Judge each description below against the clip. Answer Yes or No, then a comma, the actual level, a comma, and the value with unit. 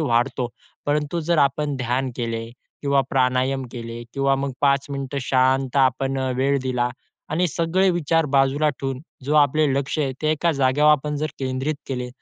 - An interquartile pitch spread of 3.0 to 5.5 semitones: No, narrow, 2.4 semitones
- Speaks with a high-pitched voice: No, low, 135 Hz